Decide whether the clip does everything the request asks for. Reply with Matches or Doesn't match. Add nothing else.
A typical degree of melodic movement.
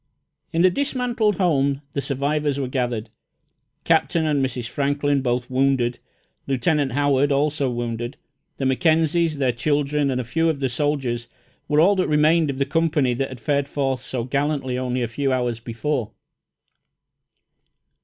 Matches